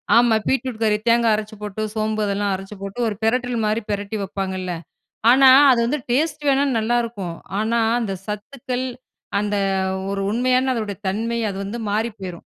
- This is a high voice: Yes, high, 220 Hz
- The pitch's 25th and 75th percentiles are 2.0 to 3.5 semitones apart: Yes, average, 3.0 semitones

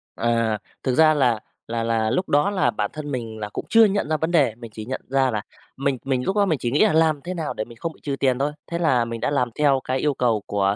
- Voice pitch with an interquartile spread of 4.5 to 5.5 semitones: Yes, average, 5.1 semitones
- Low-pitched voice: Yes, low, 130 Hz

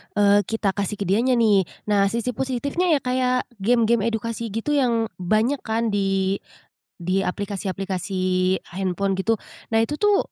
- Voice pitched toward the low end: No, high, 215 Hz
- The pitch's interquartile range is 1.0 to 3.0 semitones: No, average, 3.5 semitones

